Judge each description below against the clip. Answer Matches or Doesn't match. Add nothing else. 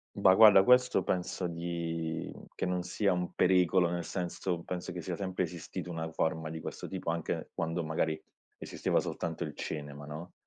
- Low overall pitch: Matches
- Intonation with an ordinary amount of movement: Doesn't match